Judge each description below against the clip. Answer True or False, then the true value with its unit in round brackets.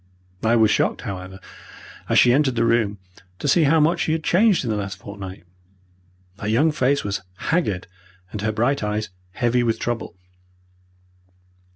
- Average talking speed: True (165 wpm)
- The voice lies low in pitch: True (115 Hz)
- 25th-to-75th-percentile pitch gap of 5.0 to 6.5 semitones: True (5.6 semitones)